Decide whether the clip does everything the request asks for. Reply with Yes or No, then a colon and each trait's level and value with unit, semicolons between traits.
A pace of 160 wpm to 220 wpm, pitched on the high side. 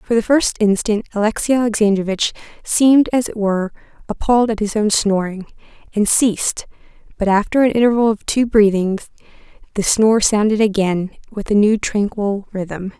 No: average, 150 wpm; high, 210 Hz